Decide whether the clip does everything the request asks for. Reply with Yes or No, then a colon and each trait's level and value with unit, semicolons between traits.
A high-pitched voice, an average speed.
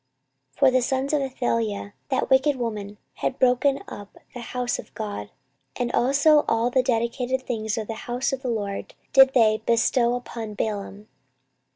Yes: high, 245 Hz; average, 170 wpm